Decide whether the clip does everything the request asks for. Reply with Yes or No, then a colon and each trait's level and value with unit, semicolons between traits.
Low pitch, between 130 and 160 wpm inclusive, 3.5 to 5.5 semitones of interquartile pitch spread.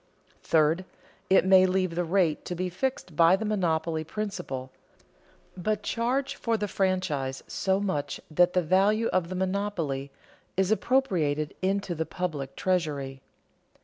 No: medium, 185 Hz; average, 140 wpm; average, 3.8 semitones